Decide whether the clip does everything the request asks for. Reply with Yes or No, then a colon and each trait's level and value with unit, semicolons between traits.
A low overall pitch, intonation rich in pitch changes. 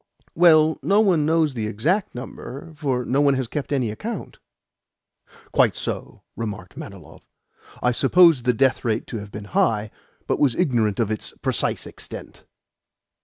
Yes: low, 130 Hz; wide, 6.1 semitones